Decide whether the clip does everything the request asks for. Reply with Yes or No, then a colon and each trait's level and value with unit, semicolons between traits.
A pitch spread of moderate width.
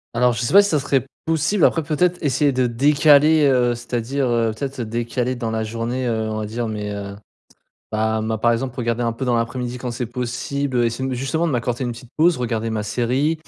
Yes: average, 3.1 semitones